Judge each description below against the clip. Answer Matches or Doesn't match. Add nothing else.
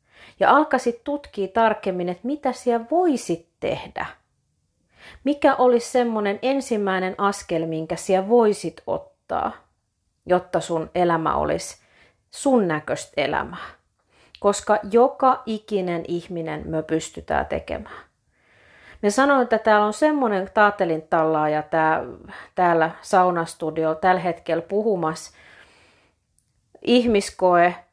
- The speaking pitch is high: Matches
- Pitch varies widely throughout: Matches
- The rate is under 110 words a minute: Matches